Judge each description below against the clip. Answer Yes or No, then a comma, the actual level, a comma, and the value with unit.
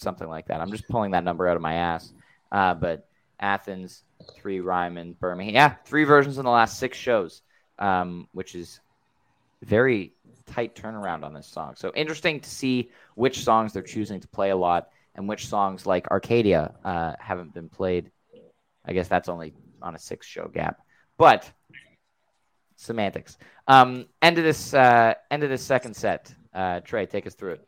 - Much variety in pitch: Yes, wide, 5.9 semitones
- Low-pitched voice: Yes, low, 100 Hz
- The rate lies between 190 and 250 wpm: No, average, 180 wpm